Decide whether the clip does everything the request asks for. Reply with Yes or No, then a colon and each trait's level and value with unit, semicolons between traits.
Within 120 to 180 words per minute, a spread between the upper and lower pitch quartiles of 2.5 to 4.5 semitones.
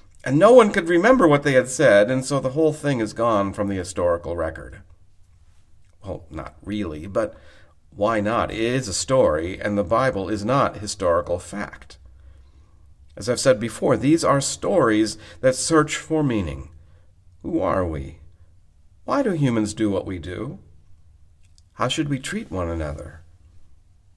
No: average, 160 wpm; average, 5.2 semitones